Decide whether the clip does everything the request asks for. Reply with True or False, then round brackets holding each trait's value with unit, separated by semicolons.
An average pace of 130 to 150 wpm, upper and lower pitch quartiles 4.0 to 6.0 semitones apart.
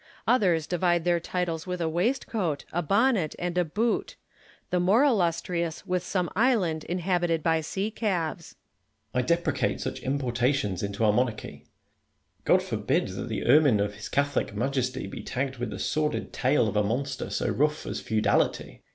False (175 wpm; 5.5 semitones)